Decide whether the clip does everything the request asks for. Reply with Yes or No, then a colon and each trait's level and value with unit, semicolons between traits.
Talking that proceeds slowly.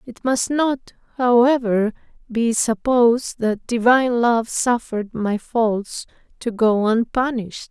Yes: slow, 115 wpm